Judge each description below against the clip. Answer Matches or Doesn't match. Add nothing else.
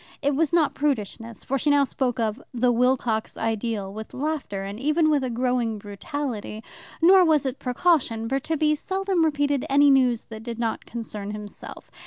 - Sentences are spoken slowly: Doesn't match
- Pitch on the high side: Matches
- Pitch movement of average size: Matches